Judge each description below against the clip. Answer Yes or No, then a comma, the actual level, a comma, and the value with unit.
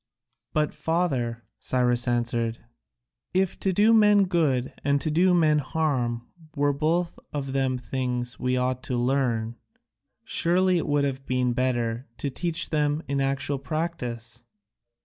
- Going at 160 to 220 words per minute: No, average, 140 wpm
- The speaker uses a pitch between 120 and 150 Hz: Yes, low, 135 Hz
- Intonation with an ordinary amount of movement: Yes, average, 4.6 semitones